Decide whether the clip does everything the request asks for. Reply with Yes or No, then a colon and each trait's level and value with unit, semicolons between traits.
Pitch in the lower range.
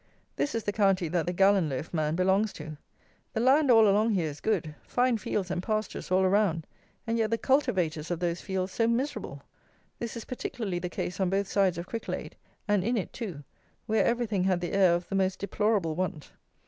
No: high, 195 Hz